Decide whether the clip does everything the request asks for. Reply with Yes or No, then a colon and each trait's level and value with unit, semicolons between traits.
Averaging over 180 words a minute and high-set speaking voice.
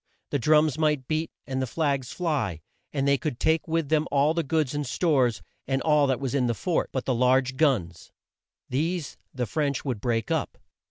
No: average, 200 wpm; medium, 140 Hz